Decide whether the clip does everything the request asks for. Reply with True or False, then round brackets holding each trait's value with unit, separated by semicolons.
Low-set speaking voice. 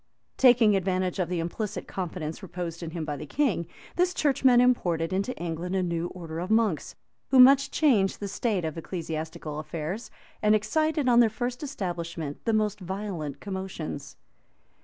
False (190 Hz)